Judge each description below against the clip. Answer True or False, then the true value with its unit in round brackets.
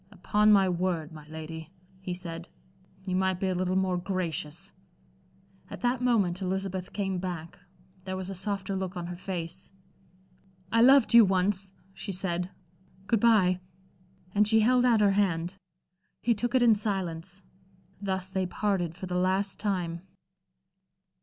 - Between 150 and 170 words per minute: True (155 wpm)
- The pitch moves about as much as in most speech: False (2.3 semitones)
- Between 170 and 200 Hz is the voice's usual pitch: True (190 Hz)